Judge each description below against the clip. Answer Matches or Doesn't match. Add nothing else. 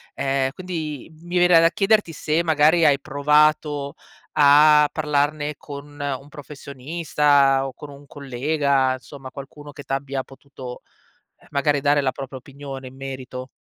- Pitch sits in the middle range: Matches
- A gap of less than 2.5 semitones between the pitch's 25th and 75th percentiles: Matches